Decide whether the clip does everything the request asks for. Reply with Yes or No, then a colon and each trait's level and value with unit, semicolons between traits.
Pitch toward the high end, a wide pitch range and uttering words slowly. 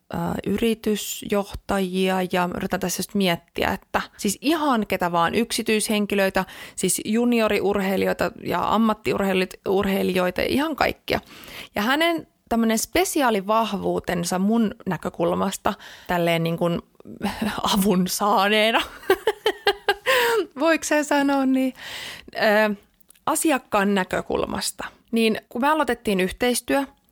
Yes: high, 210 Hz; wide, 5.8 semitones; slow, 90 wpm